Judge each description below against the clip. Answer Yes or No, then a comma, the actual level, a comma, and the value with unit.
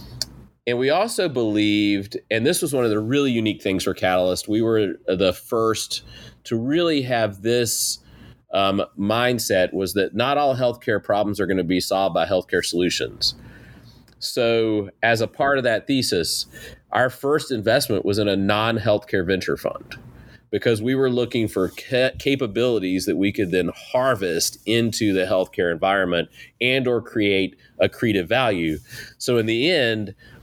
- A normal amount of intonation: Yes, average, 3.7 semitones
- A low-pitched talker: Yes, low, 110 Hz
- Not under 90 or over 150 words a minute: No, average, 160 wpm